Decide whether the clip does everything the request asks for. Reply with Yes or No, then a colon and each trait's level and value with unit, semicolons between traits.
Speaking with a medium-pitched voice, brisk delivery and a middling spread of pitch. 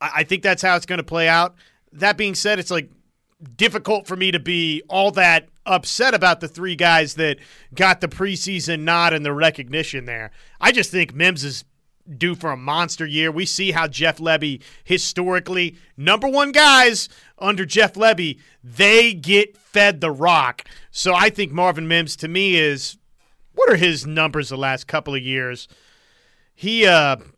No: medium, 170 Hz; average, 180 wpm; average, 3.7 semitones